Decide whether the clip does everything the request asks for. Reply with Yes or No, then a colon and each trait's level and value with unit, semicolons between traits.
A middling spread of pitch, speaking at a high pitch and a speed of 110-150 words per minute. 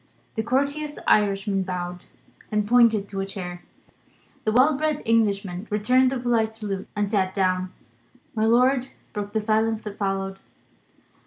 Yes: average, 3.4 semitones; high, 210 Hz; average, 145 wpm